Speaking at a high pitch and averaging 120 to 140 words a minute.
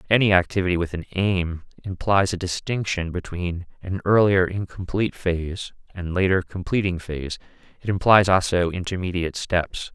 No: very low, 90 Hz; slow, 135 wpm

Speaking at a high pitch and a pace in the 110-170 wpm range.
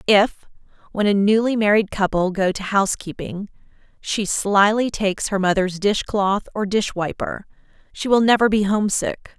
Yes: high, 205 Hz; average, 155 wpm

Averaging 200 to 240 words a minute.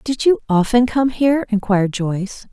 No: average, 165 wpm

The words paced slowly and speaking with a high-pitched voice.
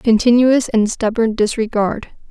Yes: slow, 105 wpm; high, 225 Hz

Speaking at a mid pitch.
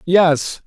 Yes: medium, 160 Hz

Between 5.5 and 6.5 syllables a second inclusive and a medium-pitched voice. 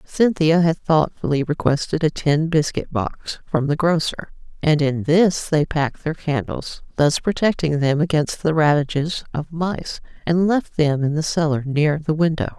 No: 4.4 syllables/s; medium, 155 Hz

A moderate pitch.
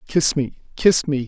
Yes: medium, 145 Hz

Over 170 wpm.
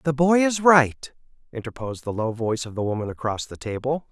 Yes: fast, 205 wpm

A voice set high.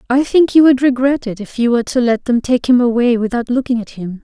Yes: high, 245 Hz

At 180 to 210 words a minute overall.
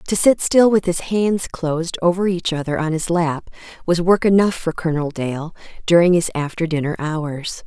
Yes: average, 190 wpm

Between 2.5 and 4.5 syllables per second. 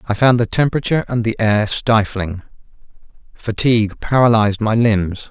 No: 5.2 syllables/s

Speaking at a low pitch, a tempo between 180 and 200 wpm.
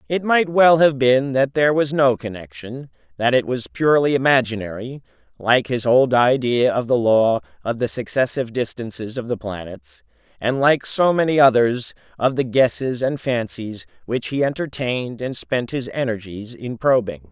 No: low, 125 Hz; average, 165 wpm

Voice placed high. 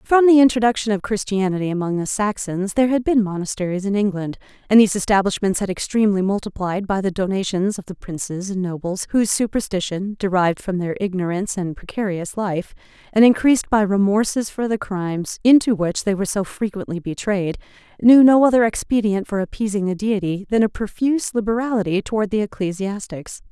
Yes: high, 200 Hz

